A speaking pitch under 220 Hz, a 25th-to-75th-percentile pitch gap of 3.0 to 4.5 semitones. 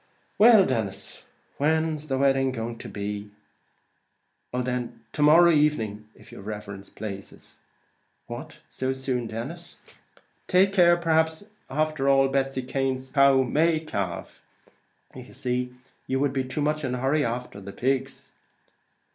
Yes: low, 135 Hz; average, 3.9 semitones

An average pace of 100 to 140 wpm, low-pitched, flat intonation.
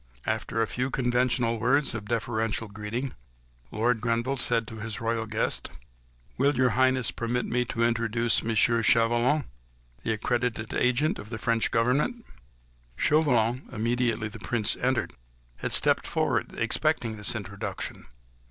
Yes: slow, 135 wpm; low, 115 Hz; narrow, 2.0 semitones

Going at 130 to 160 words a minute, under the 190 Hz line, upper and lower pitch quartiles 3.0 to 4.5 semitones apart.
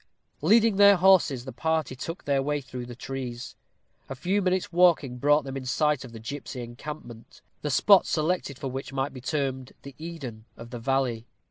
No: average, 190 wpm; low, 135 Hz; average, 4.2 semitones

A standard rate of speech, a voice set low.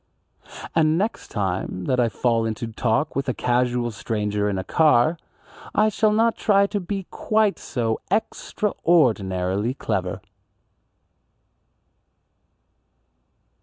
No: slow, 110 wpm; low, 125 Hz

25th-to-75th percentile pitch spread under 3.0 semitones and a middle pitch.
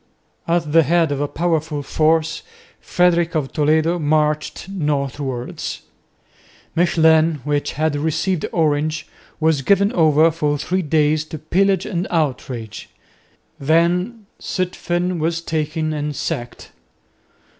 Yes: narrow, 2.4 semitones; medium, 160 Hz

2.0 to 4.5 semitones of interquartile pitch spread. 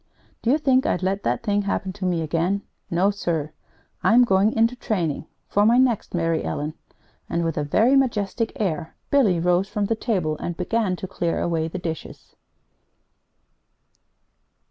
No: average, 4.9 semitones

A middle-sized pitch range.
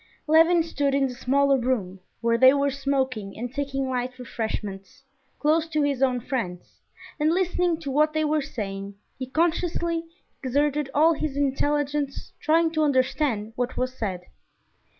Yes: average, 3.6 semitones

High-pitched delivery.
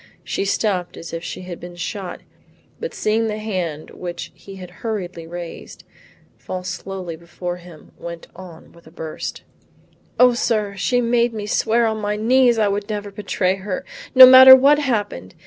Yes: high, 200 Hz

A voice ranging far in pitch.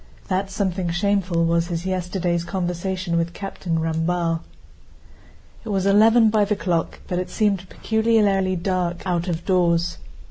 No: narrow, 2.4 semitones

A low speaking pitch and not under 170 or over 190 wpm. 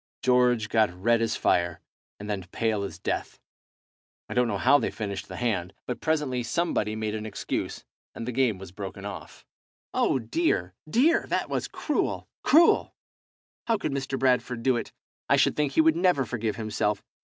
Yes: low, 115 Hz; average, 180 wpm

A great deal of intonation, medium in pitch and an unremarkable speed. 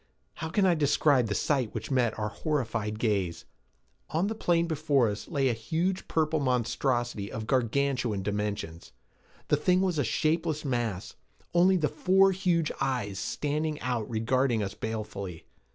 No: wide, 6.4 semitones; low, 130 Hz; average, 150 wpm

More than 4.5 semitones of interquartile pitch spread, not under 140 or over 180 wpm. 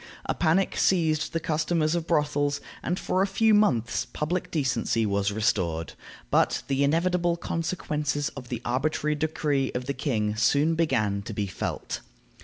Yes: wide, 5.5 semitones; average, 155 wpm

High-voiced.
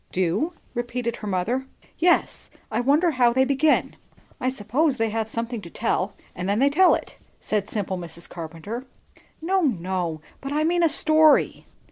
Yes: high, 240 Hz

